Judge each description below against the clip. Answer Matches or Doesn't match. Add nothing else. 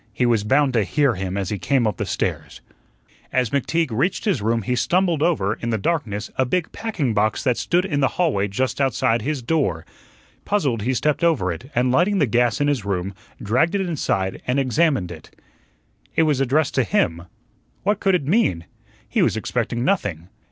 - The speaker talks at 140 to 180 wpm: Doesn't match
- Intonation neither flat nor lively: Doesn't match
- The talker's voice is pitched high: Doesn't match